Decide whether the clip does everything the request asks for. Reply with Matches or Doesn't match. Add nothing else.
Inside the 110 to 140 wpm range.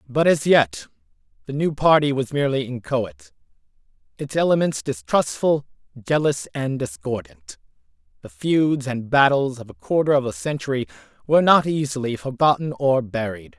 Matches